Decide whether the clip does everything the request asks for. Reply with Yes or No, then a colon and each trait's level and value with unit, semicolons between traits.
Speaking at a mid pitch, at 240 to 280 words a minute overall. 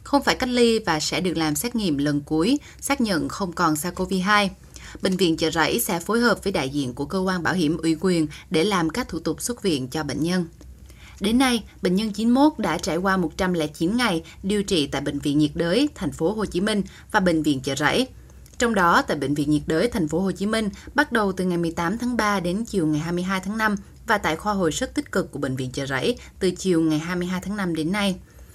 Yes: medium, 180 Hz; average, 245 wpm